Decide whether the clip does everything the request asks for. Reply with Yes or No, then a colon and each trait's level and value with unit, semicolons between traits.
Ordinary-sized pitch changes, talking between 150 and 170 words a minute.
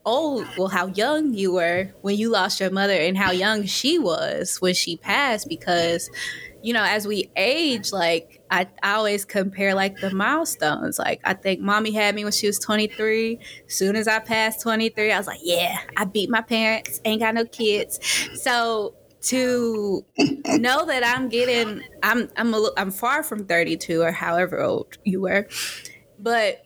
No: average, 3.2 semitones; average, 180 wpm